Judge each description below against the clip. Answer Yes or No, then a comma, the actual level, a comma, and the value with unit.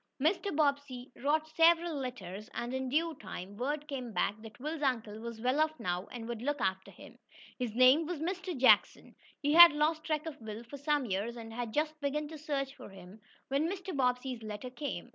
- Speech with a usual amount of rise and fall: Yes, average, 5.0 semitones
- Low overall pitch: No, very high, 270 Hz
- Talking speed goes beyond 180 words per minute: Yes, average, 200 wpm